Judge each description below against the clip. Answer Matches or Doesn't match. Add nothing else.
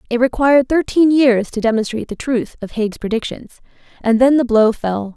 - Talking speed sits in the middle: Matches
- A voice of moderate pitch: Doesn't match